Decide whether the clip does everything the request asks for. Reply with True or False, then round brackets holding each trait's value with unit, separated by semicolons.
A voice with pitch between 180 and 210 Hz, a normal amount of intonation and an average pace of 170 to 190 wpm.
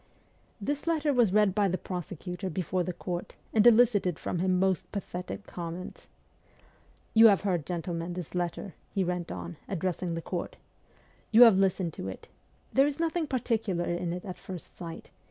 True (185 Hz; 3.4 semitones; 180 wpm)